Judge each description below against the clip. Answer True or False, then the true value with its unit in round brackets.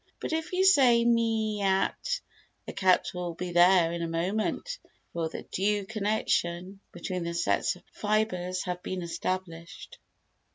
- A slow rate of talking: False (155 wpm)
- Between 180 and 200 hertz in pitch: True (185 Hz)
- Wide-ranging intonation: False (3.9 semitones)